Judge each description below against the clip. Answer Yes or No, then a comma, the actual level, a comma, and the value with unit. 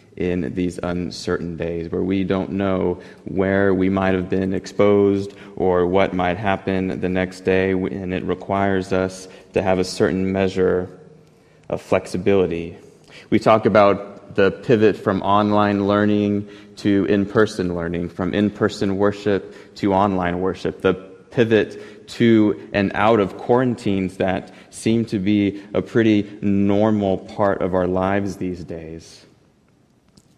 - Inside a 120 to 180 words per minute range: Yes, average, 140 wpm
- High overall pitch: No, very low, 95 Hz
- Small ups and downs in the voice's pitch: Yes, narrow, 1.7 semitones